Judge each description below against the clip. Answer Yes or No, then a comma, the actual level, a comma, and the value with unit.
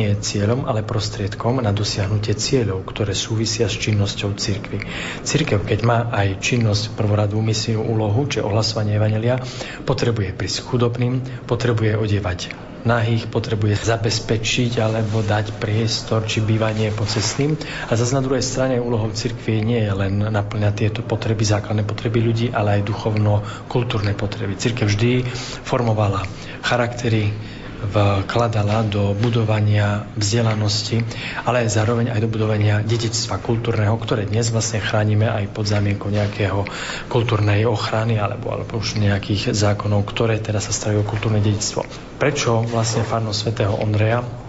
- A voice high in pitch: No, low, 110 Hz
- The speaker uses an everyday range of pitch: No, narrow, 2.1 semitones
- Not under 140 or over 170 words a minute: No, average, 130 wpm